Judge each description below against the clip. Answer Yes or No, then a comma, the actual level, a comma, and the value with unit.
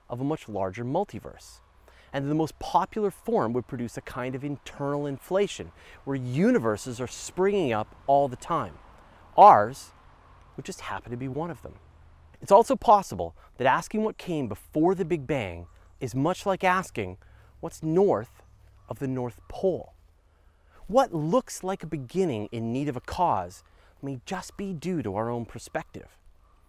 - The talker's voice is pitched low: Yes, low, 130 Hz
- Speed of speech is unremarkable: Yes, average, 165 wpm